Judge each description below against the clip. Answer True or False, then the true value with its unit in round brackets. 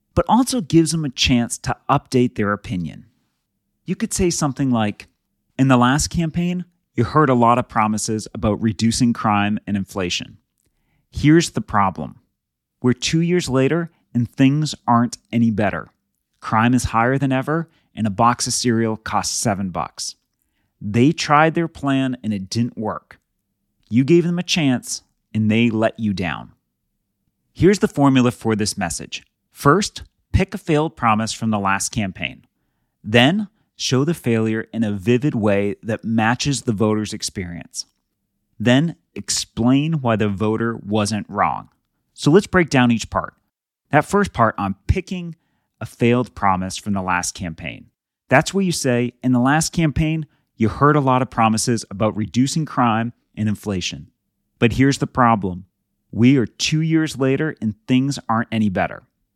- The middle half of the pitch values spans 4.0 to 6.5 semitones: True (5.1 semitones)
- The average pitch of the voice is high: False (120 Hz)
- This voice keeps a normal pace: True (160 wpm)